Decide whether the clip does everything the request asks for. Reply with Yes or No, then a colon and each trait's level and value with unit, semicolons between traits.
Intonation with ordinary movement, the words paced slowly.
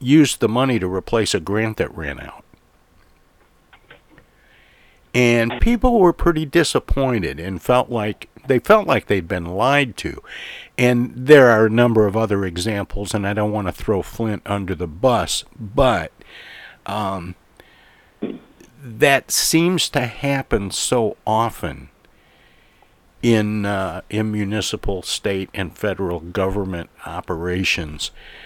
Yes: average, 4.7 semitones; slow, 125 wpm